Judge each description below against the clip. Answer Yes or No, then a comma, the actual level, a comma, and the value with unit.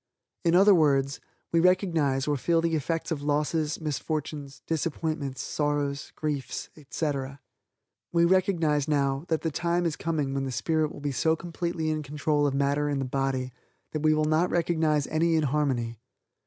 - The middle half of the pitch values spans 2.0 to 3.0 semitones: Yes, average, 2.7 semitones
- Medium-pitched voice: Yes, medium, 150 Hz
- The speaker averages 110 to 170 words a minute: Yes, average, 165 wpm